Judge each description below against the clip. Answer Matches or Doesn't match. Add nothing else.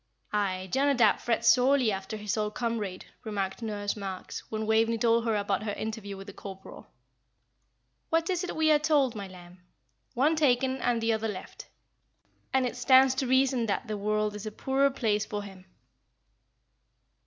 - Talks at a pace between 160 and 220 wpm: Matches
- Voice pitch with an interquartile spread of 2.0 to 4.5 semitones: Matches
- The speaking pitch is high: Matches